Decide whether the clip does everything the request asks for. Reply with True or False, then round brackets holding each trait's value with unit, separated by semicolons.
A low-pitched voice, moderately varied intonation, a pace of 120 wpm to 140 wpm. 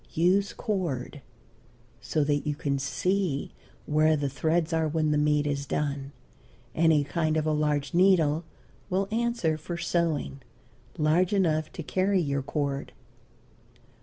False (155 Hz; 3.0 semitones; 135 wpm)